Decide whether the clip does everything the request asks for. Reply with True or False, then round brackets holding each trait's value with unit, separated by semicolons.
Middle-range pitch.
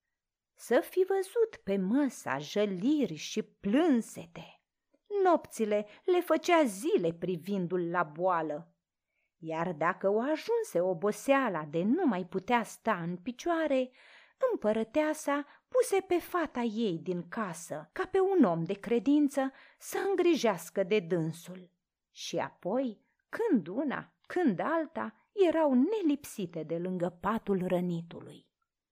False (230 Hz)